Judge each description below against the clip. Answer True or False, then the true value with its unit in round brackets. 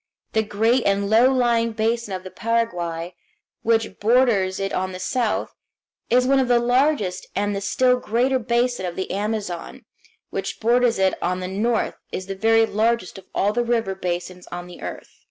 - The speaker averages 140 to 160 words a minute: False (180 wpm)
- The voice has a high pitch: True (220 Hz)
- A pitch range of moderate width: True (4.1 semitones)